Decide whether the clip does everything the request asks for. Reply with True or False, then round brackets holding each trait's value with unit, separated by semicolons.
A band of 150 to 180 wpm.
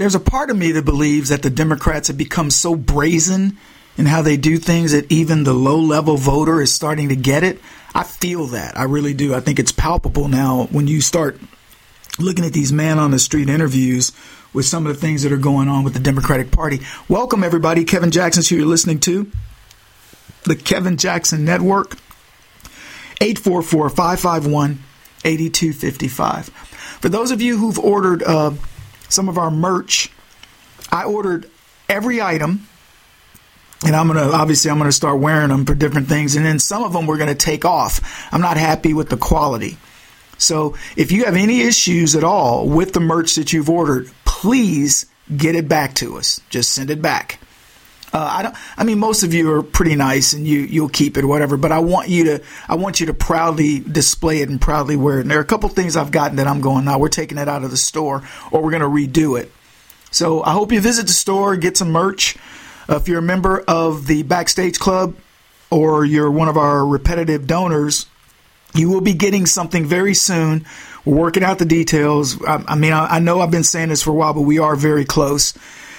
False (205 wpm)